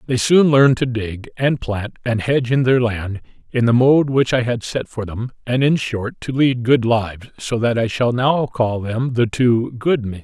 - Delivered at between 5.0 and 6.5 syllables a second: No, 4.5 syllables/s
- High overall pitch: No, low, 120 Hz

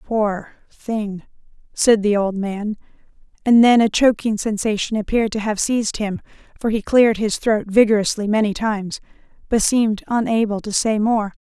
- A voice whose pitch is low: No, high, 215 Hz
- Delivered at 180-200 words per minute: No, average, 155 wpm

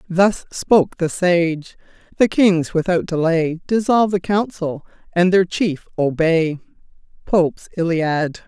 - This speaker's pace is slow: Yes, slow, 120 wpm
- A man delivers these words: No, female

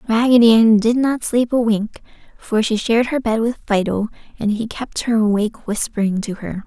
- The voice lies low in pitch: No, high, 225 Hz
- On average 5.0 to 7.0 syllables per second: Yes, 5.1 syllables/s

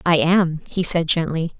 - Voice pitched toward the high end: No, medium, 170 Hz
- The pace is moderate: Yes, average, 190 wpm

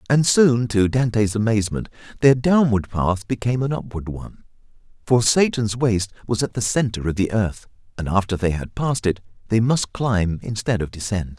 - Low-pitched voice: Yes, low, 110 Hz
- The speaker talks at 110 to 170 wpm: No, average, 180 wpm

